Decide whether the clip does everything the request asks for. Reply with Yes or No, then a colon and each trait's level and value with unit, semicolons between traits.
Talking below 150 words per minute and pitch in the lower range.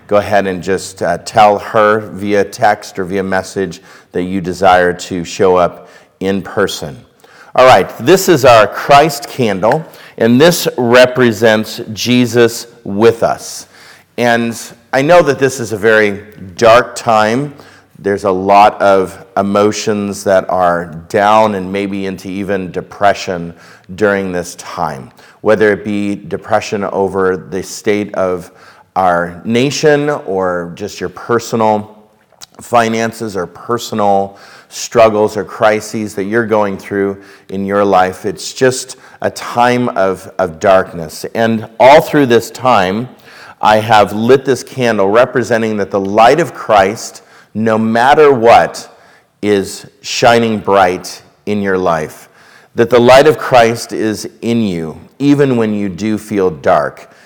Yes: average, 140 wpm; low, 105 Hz